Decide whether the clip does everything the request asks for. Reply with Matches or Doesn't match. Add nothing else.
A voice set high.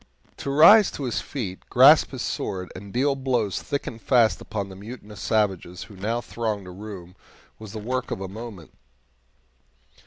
Doesn't match